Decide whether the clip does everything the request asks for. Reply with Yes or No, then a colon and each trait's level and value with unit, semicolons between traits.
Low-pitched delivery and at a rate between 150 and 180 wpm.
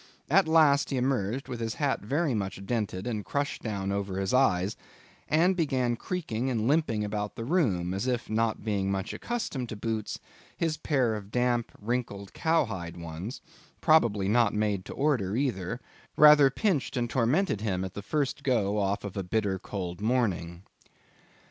Yes: low, 115 Hz; average, 160 wpm